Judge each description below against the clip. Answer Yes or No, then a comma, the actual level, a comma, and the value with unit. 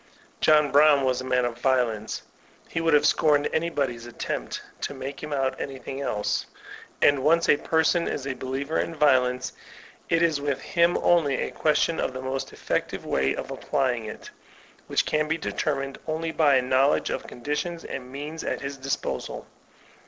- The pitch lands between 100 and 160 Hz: Yes, medium, 140 Hz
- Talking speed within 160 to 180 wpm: Yes, average, 175 wpm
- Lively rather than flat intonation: No, average, 2.9 semitones